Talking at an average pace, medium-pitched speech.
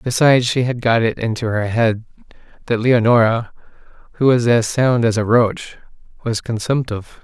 No: average, 160 wpm; low, 115 Hz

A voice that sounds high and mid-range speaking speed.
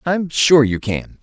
No: medium, 140 Hz; average, 195 wpm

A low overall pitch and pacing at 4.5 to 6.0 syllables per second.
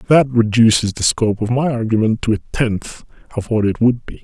Yes: low, 115 Hz; 5.3 syllables/s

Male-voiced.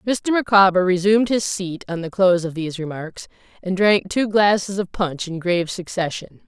No: female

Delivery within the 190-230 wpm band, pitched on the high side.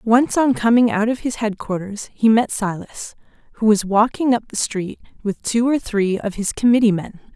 Yes: average, 195 wpm; high, 220 Hz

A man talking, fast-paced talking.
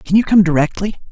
Yes: male; fast, 215 wpm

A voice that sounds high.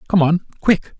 No: medium, 175 Hz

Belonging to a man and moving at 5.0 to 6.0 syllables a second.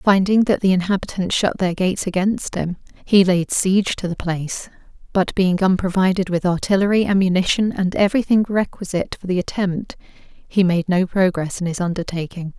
No: female; 5.3 syllables/s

